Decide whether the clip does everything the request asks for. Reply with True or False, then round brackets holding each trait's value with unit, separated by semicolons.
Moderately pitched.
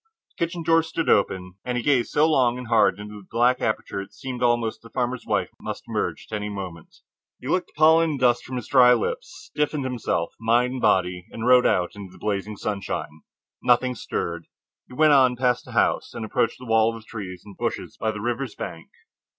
False (120 Hz)